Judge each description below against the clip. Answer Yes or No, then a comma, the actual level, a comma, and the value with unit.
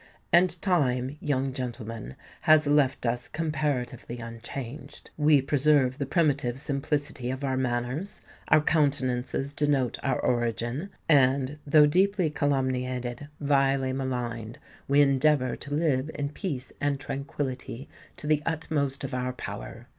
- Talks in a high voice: No, low, 135 Hz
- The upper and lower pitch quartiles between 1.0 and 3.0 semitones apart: Yes, average, 2.7 semitones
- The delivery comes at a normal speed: No, slow, 125 wpm